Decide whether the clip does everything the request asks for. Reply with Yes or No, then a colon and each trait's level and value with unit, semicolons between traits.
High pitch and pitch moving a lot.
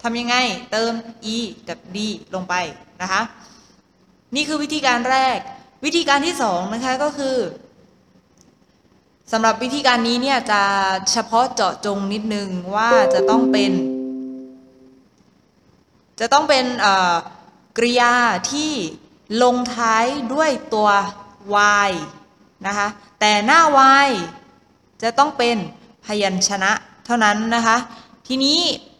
No: high, 225 Hz; average, 4.2 semitones